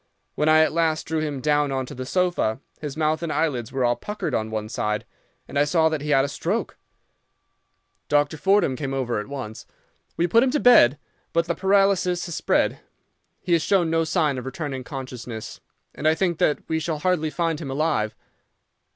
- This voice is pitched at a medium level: Yes, medium, 155 Hz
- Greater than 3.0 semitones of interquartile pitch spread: Yes, average, 4.1 semitones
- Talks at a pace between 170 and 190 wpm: No, average, 200 wpm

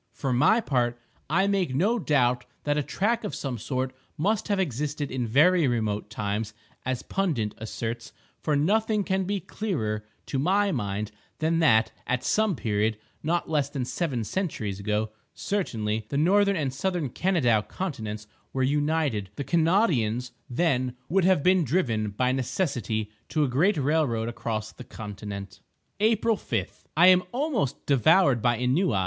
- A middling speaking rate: Yes, average, 150 wpm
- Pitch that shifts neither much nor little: No, wide, 8.2 semitones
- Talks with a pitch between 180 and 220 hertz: No, low, 135 Hz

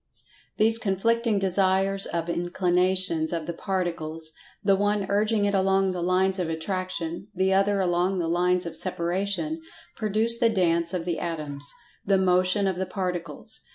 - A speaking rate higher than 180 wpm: No, slow, 135 wpm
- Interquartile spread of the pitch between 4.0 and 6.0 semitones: No, narrow, 2.4 semitones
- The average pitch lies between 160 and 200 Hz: Yes, medium, 185 Hz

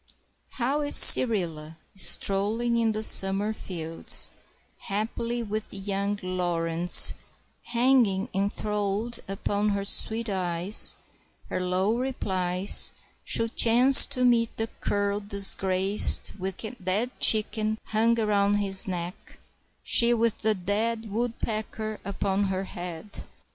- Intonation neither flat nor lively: Yes, average, 3.0 semitones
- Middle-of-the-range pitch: No, high, 205 Hz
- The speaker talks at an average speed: No, slow, 110 wpm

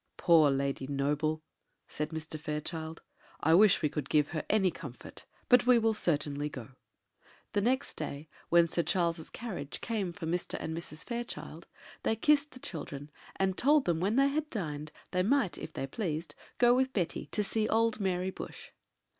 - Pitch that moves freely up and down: Yes, wide, 6.5 semitones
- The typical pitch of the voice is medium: Yes, medium, 175 Hz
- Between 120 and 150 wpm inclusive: No, average, 175 wpm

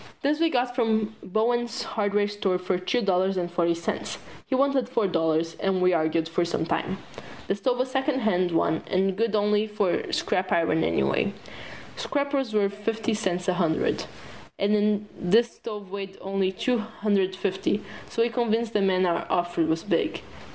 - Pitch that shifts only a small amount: No, average, 3.8 semitones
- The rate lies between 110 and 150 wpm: No, average, 175 wpm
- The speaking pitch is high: Yes, high, 200 Hz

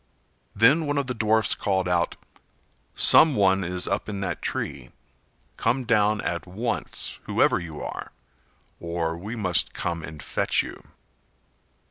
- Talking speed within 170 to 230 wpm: No, average, 140 wpm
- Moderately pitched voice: No, low, 100 Hz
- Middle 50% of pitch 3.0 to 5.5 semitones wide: Yes, average, 4.7 semitones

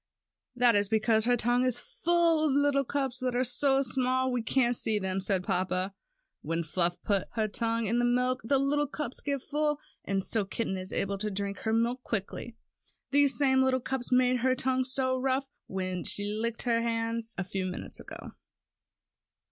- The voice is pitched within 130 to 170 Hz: No, high, 240 Hz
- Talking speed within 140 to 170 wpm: No, average, 190 wpm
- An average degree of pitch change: Yes, average, 4.4 semitones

